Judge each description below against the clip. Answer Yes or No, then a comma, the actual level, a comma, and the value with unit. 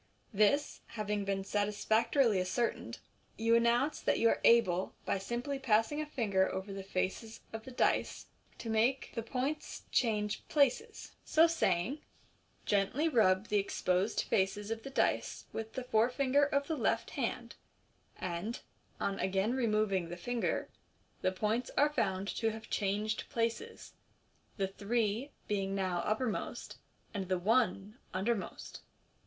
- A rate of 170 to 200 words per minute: No, average, 145 wpm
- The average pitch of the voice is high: Yes, high, 220 Hz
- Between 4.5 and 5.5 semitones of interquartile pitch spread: No, average, 4.0 semitones